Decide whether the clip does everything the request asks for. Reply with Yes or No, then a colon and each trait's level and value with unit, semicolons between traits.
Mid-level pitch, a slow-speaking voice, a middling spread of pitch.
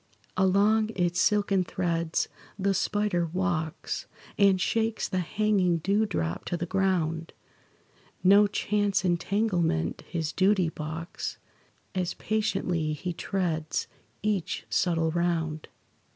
Yes: medium, 180 Hz; slow, 110 wpm; average, 3.2 semitones